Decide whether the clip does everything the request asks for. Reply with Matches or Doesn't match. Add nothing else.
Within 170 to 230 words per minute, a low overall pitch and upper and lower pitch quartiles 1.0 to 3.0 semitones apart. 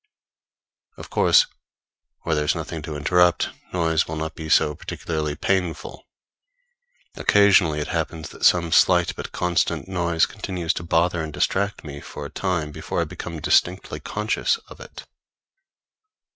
Doesn't match